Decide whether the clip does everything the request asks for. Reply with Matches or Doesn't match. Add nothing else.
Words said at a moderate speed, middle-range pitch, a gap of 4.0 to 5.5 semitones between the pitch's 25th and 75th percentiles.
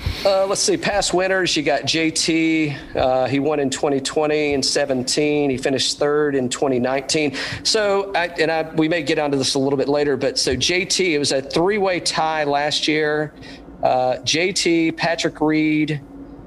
Doesn't match